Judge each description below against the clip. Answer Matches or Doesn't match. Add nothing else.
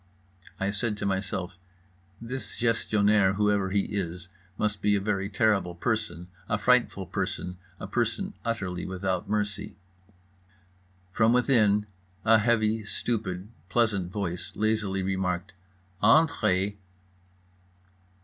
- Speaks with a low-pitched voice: Matches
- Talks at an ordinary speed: Doesn't match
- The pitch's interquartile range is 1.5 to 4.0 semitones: Matches